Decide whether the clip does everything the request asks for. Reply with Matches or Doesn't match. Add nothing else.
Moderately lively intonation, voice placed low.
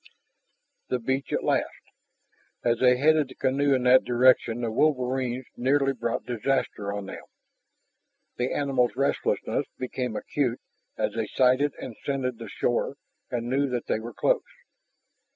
Doesn't match